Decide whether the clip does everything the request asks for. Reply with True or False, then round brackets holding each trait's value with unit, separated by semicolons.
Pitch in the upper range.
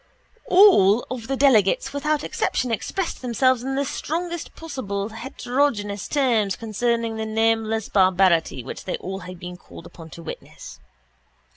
True (225 Hz)